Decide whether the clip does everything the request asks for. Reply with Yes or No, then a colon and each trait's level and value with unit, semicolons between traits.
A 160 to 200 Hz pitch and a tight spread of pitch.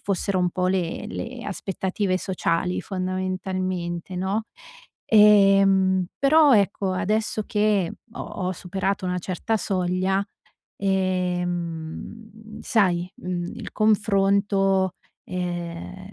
Yes: high, 190 Hz; narrow, 1.9 semitones